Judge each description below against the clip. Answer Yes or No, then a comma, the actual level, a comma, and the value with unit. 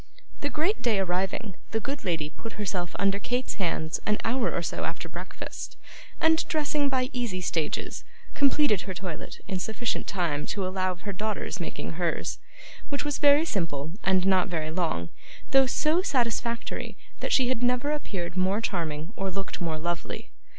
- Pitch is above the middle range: Yes, high, 195 Hz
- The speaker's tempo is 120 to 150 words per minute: No, average, 170 wpm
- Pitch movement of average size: No, wide, 6.1 semitones